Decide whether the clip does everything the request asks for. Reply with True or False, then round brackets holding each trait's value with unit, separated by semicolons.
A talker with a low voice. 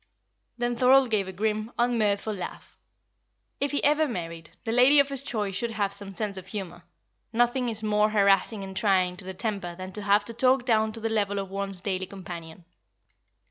False (210 Hz)